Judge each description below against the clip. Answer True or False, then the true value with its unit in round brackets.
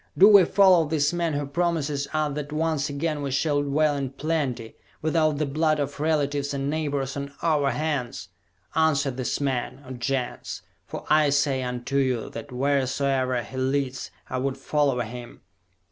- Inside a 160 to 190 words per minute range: True (165 wpm)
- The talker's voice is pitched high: False (140 Hz)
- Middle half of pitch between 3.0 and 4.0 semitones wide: False (2.6 semitones)